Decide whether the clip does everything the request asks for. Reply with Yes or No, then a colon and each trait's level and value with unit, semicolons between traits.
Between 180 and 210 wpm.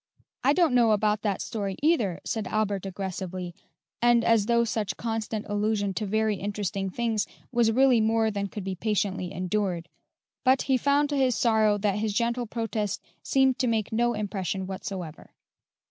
No: average, 165 wpm